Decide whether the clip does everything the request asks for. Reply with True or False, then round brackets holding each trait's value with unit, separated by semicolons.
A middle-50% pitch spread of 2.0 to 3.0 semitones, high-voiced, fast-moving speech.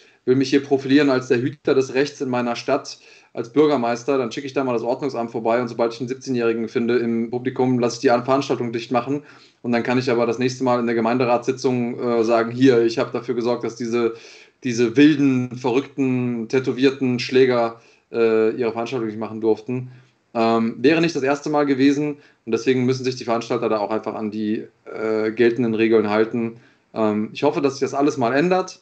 False (2.6 semitones; 125 Hz; 205 wpm)